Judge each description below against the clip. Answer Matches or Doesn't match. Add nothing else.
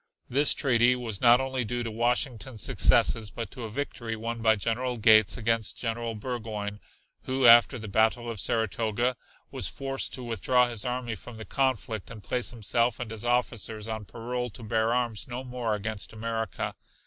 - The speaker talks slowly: Doesn't match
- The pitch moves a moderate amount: Doesn't match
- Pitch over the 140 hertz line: Doesn't match